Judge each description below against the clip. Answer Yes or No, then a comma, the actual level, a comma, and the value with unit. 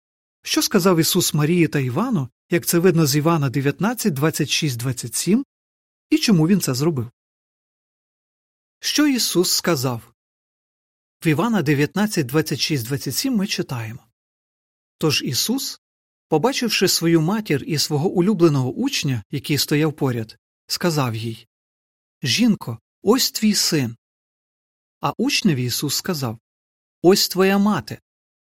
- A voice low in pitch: No, medium, 160 Hz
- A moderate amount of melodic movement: No, wide, 7.2 semitones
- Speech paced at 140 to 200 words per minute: No, average, 115 wpm